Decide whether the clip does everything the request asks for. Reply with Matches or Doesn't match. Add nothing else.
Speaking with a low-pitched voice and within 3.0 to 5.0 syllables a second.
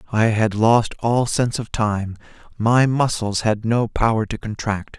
Matches